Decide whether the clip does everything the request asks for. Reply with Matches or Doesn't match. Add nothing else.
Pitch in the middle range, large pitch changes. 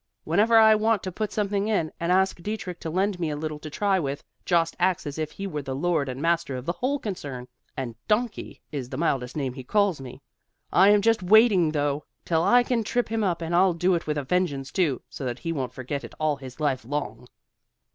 Matches